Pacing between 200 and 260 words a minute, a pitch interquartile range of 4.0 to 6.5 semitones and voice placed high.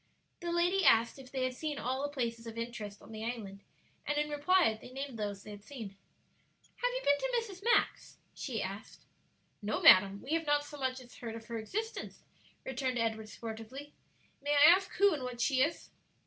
Yes: fast, 205 wpm; average, 4.9 semitones; very high, 255 Hz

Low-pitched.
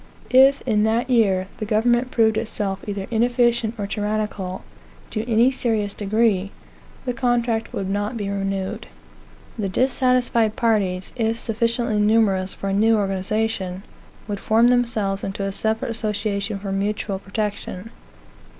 No: high, 215 Hz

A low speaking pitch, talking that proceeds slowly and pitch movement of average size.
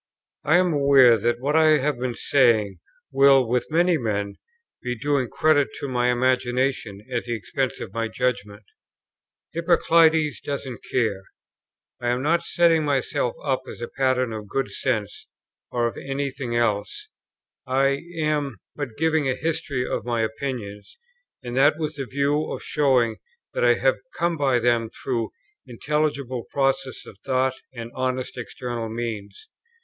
No: low, 130 Hz; average, 155 wpm; average, 3.5 semitones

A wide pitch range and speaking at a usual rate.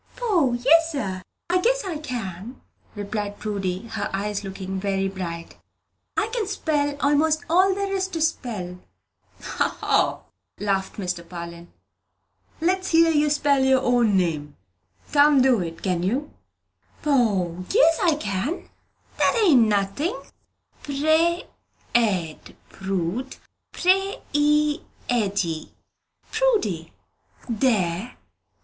No: wide, 8.5 semitones; slow, 115 wpm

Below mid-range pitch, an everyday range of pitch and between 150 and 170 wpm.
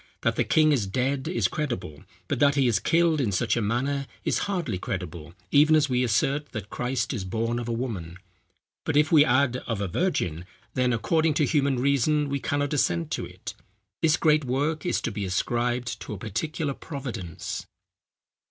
No: low, 130 Hz; average, 5.0 semitones; average, 190 wpm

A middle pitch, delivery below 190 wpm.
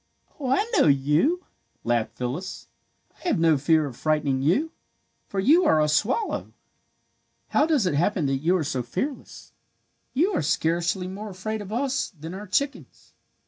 Yes: medium, 180 Hz; average, 165 wpm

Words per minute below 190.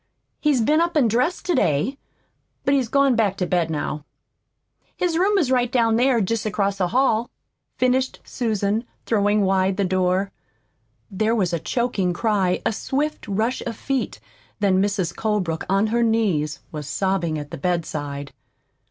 Yes: average, 160 wpm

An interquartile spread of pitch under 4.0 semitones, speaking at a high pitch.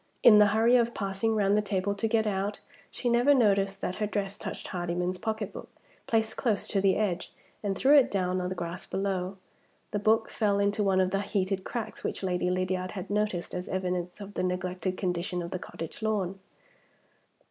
Yes: narrow, 2.5 semitones; high, 195 Hz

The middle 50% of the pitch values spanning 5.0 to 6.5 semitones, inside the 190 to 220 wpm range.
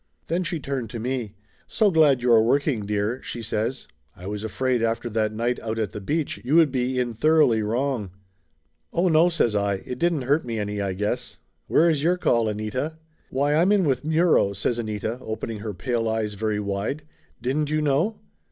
Yes: wide, 5.5 semitones; average, 200 wpm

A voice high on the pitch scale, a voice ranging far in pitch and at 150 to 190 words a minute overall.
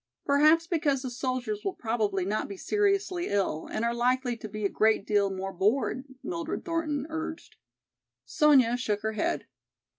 Yes: very high, 255 Hz; wide, 7.1 semitones; average, 160 wpm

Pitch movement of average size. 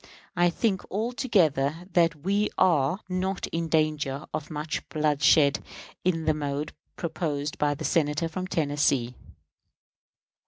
Yes: average, 3.6 semitones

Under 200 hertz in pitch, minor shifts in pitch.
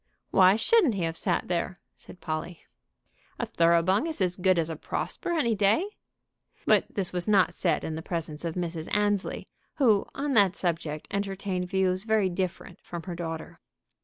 No: medium, 185 Hz; average, 3.1 semitones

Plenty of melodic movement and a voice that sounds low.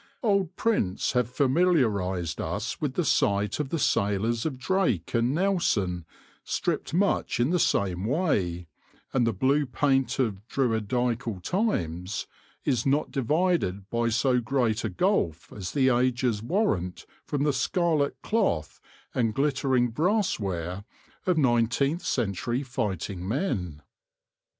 Yes: wide, 6.7 semitones; low, 125 Hz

